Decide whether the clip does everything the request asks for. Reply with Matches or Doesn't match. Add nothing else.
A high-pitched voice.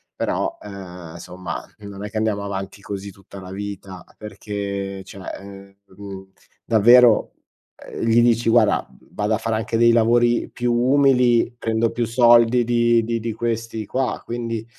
Doesn't match